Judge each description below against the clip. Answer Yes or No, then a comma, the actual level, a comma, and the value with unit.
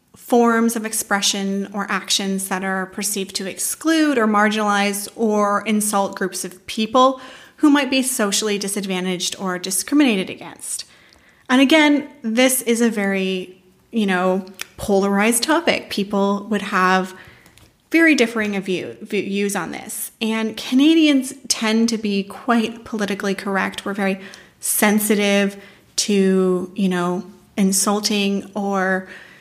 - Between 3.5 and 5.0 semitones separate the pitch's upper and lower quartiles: No, average, 3.0 semitones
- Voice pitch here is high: Yes, high, 205 Hz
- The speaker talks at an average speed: No, slow, 120 wpm